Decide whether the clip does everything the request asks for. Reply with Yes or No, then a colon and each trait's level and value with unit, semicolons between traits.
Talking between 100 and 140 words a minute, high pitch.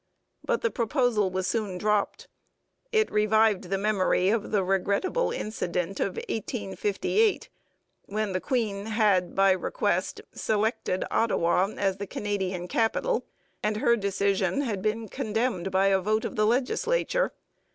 Yes: slow, 135 wpm; high, 210 Hz